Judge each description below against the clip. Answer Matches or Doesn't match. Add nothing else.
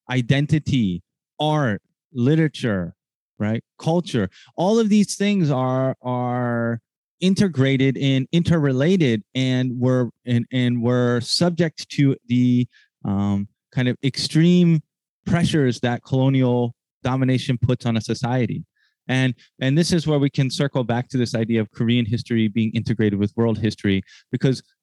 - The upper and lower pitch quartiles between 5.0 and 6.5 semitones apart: Doesn't match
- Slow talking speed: Matches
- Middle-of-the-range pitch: Doesn't match